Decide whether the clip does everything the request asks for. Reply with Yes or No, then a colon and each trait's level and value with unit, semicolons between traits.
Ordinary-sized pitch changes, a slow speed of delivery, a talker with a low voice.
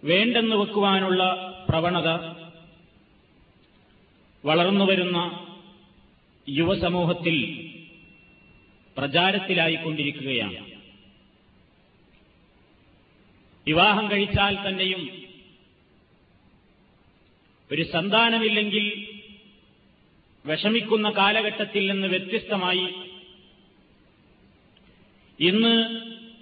No: average, 4.1 semitones; slow, 35 wpm; medium, 185 Hz